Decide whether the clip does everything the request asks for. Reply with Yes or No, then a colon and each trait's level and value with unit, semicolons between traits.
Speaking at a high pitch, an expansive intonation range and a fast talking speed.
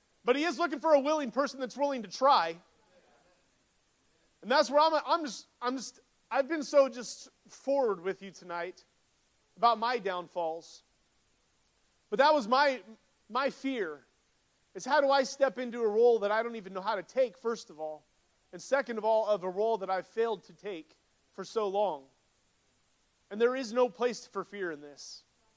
No: high, 230 Hz; wide, 6.3 semitones; average, 190 wpm